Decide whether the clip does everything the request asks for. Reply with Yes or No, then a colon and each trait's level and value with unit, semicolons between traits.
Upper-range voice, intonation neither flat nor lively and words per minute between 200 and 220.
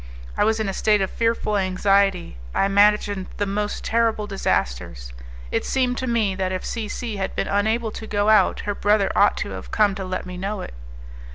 No: high, 205 Hz; narrow, 2.2 semitones; fast, 205 wpm